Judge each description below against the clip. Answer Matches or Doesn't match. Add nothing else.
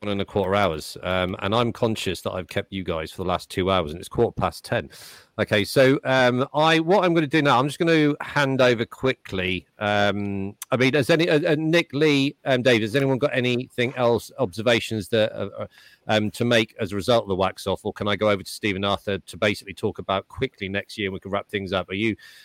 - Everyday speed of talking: Doesn't match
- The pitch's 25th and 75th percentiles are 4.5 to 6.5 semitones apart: Matches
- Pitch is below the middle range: Matches